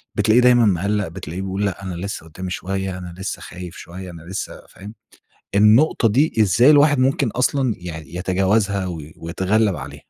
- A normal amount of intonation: Yes, average, 3.7 semitones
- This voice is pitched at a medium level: No, very low, 95 Hz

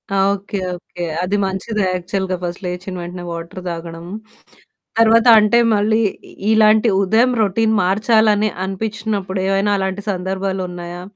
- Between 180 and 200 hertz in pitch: Yes, high, 195 Hz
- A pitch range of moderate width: Yes, average, 3.0 semitones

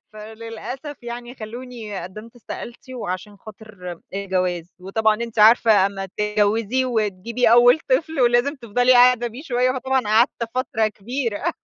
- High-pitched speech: Yes, high, 230 Hz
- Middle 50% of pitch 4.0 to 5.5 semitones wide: No, average, 2.9 semitones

